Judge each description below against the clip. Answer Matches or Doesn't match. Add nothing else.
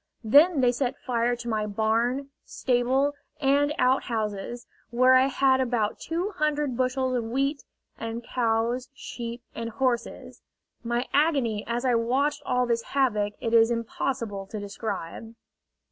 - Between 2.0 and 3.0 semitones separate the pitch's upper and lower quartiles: Matches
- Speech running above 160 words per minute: Doesn't match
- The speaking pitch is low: Doesn't match